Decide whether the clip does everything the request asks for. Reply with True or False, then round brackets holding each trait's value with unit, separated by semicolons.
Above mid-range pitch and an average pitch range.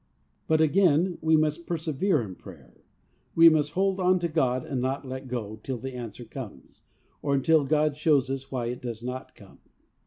False (140 Hz; 4.1 semitones)